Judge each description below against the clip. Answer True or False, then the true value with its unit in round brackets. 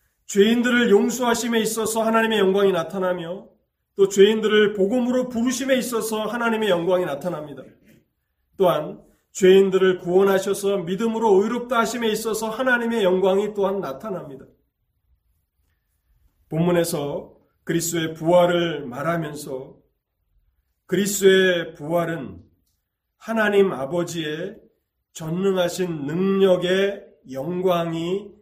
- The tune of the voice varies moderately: True (4.4 semitones)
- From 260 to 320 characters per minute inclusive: True (275 characters per minute)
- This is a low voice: False (190 Hz)